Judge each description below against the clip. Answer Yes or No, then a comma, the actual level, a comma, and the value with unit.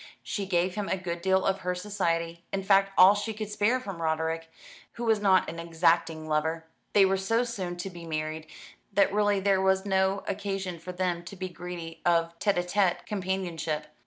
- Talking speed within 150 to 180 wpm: No, average, 195 wpm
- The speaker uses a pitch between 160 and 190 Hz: Yes, medium, 185 Hz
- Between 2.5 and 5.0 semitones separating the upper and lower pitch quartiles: Yes, average, 2.8 semitones